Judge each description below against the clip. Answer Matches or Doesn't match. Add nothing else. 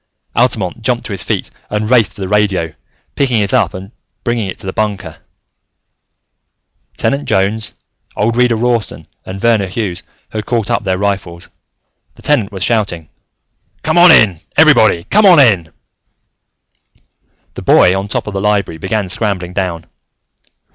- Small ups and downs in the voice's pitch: Doesn't match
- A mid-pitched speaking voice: Doesn't match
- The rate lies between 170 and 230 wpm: Doesn't match